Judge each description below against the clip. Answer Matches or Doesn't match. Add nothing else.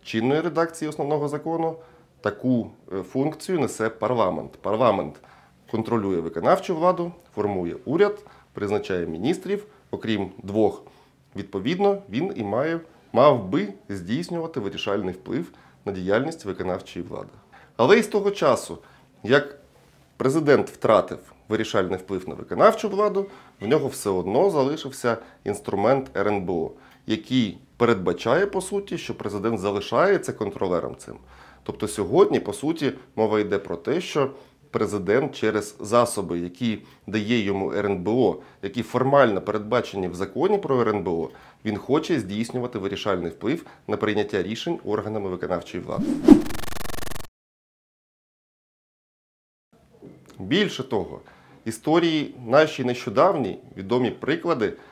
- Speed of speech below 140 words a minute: Matches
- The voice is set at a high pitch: Doesn't match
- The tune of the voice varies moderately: Doesn't match